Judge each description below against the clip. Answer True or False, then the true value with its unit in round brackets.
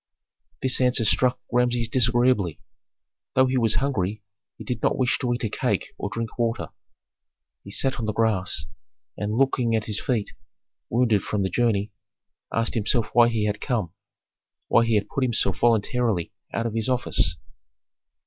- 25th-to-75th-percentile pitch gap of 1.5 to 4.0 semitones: True (2.7 semitones)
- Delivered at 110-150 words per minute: False (165 wpm)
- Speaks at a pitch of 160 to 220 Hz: False (115 Hz)